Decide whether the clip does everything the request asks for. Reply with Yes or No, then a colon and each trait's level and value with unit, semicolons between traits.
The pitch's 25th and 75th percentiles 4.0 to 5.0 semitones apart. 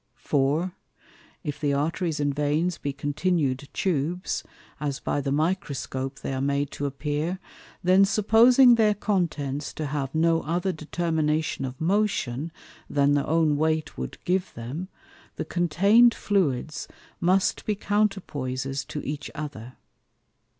Yes: average, 4.4 semitones